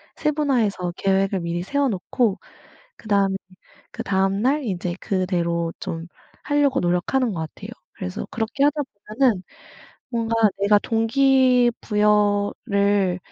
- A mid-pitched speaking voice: No, high, 205 Hz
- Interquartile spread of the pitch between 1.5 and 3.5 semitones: No, average, 5.1 semitones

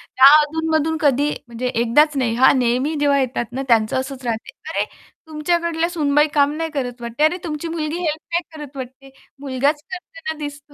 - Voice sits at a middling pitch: No, very high, 290 Hz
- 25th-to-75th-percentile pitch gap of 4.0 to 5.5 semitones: No, average, 3.4 semitones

